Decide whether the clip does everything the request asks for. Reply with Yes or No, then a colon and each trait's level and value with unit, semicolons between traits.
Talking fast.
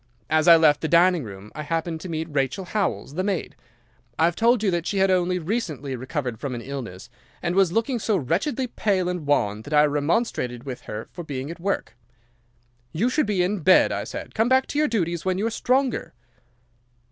Yes: fast, 210 wpm